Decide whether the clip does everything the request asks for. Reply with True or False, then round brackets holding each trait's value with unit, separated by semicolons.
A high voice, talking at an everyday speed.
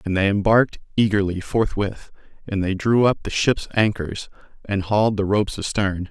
False (100 Hz; 165 wpm)